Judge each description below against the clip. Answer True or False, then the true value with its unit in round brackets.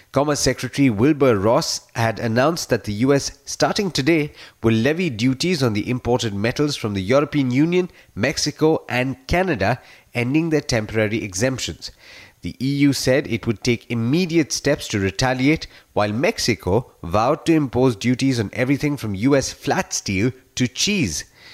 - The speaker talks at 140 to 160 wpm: True (150 wpm)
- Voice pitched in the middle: False (130 Hz)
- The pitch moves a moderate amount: True (4.4 semitones)